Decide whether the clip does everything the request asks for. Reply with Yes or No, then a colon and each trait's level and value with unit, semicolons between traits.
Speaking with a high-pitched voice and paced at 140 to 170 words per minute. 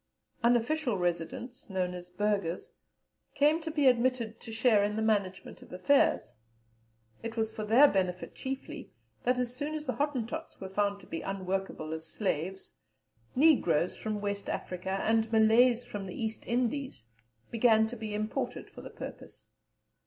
Yes: high, 220 Hz; average, 155 wpm